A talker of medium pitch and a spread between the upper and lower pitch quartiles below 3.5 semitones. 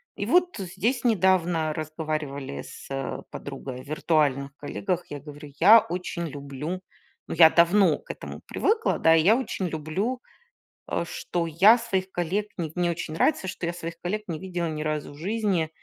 No: medium, 170 Hz; average, 3.8 semitones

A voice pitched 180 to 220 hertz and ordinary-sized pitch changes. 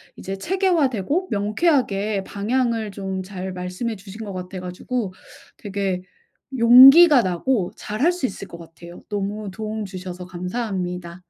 Yes: high, 200 Hz; average, 4.5 semitones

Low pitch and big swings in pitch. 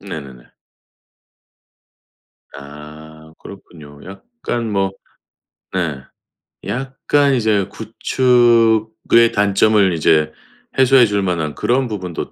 Yes: low, 100 Hz; wide, 6.8 semitones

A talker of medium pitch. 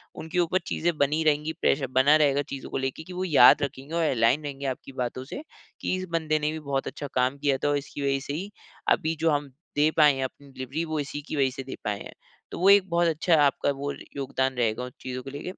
Yes: medium, 145 Hz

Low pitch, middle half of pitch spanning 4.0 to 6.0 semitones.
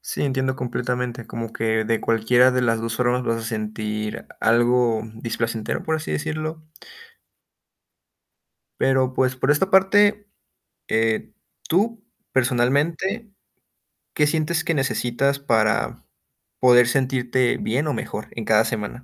Yes: low, 125 Hz; average, 4.4 semitones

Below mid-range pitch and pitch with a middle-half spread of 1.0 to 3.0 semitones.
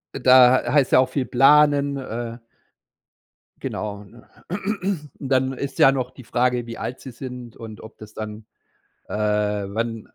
No: low, 125 Hz; average, 3.5 semitones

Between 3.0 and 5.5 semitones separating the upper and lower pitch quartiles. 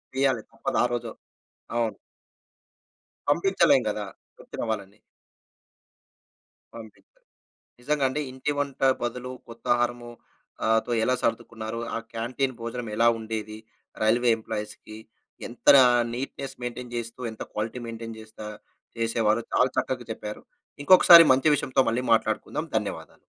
No: narrow, 2.4 semitones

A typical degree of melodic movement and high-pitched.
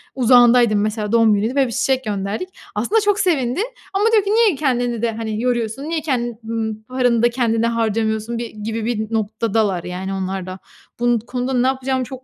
Yes: average, 3.1 semitones; high, 235 Hz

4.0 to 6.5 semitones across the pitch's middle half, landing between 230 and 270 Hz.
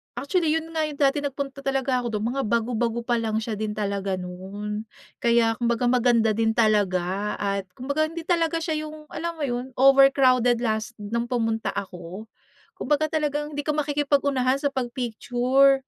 Yes: average, 4.5 semitones; very high, 250 Hz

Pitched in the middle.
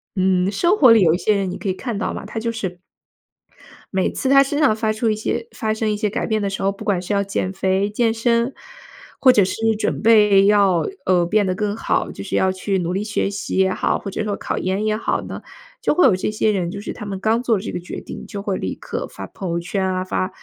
No: high, 205 Hz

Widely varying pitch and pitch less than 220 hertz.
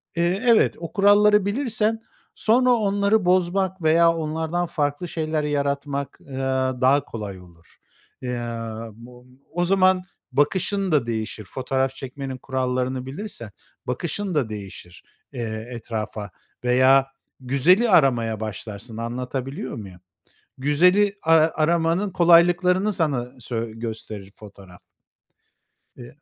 Yes: wide, 7.0 semitones; medium, 140 Hz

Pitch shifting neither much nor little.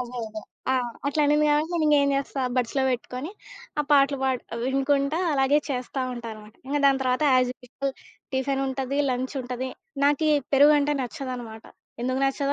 No: narrow, 2.1 semitones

